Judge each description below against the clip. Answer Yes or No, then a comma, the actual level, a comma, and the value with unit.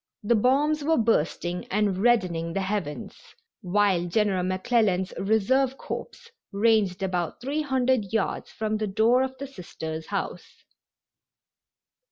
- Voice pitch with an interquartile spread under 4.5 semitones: No, average, 5.1 semitones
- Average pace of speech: No, slow, 125 wpm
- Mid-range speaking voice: No, high, 210 Hz